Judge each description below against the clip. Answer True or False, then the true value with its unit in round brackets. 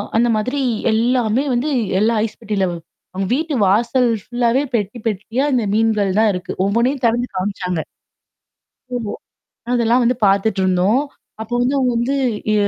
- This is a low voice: False (230 Hz)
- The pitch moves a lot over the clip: False (3.6 semitones)